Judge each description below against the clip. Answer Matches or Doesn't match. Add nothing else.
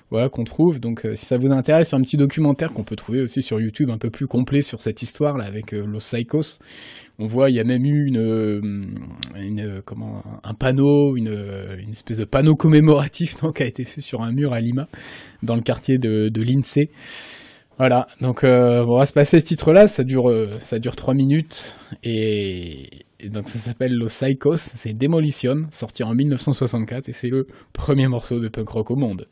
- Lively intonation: Doesn't match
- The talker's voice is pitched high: Doesn't match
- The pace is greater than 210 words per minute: Doesn't match